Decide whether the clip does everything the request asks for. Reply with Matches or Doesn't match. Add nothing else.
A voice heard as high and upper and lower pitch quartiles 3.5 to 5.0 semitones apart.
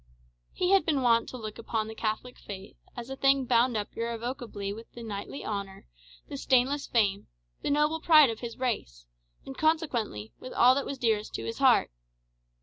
Matches